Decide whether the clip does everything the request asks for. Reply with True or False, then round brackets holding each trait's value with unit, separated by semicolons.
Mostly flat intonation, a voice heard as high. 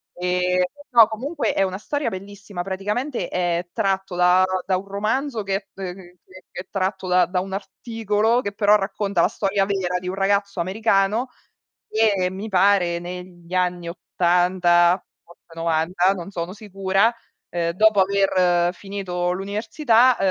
True (2.3 semitones; 195 Hz)